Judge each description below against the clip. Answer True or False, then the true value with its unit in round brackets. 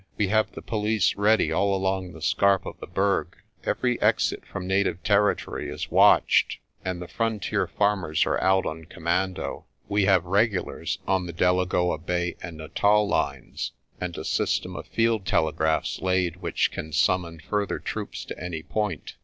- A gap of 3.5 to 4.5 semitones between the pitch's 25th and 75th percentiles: False (2.7 semitones)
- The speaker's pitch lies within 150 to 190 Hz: False (95 Hz)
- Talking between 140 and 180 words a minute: True (160 wpm)